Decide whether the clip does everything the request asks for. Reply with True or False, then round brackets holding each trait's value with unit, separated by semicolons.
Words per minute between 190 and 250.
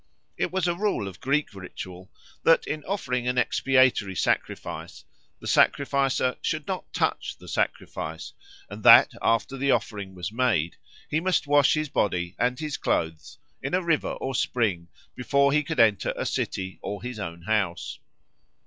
False (160 wpm)